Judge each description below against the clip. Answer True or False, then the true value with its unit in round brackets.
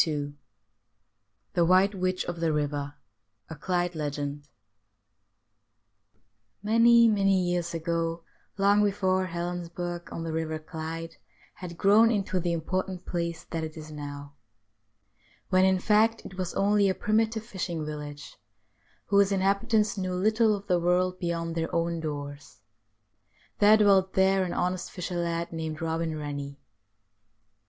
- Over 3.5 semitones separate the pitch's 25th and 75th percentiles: False (3.2 semitones)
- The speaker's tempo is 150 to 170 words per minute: False (135 wpm)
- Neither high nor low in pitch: True (175 Hz)